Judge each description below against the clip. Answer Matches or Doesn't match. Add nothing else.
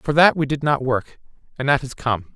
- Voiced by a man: Matches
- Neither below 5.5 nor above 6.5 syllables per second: Doesn't match